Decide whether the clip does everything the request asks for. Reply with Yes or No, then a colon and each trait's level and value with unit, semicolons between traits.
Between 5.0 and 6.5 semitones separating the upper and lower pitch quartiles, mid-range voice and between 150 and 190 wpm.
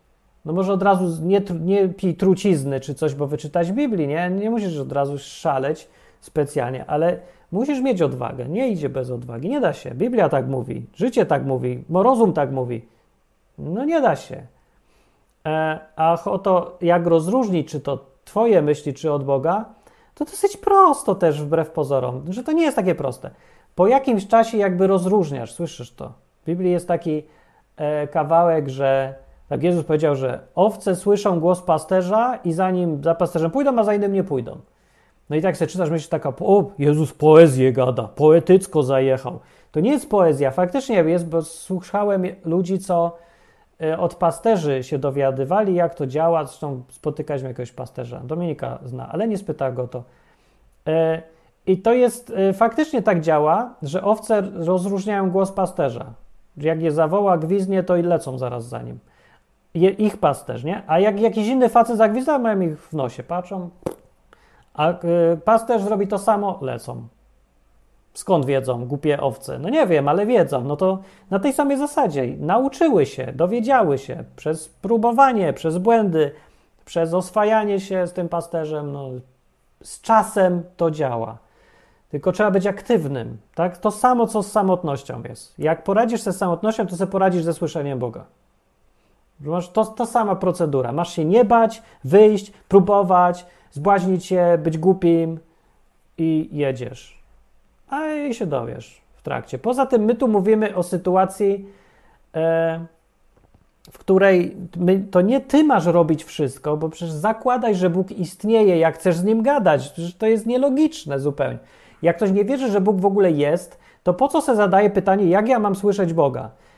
Yes: wide, 5.4 semitones; medium, 175 Hz; fast, 160 wpm